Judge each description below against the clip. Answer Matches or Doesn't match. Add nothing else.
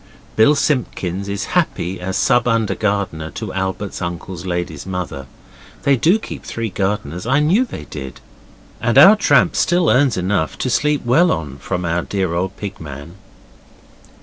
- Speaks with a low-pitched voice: Matches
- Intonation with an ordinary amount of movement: Doesn't match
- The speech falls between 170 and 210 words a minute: Doesn't match